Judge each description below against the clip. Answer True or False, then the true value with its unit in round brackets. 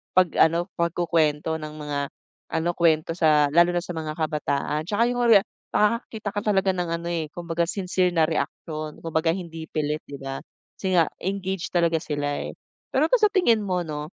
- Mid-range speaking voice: True (170 Hz)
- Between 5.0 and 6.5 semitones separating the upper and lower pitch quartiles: False (3.3 semitones)